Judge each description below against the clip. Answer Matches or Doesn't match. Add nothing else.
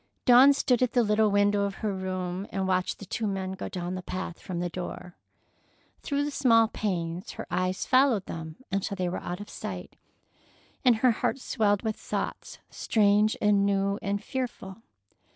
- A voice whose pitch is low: Doesn't match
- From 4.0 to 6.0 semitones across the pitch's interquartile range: Doesn't match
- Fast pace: Doesn't match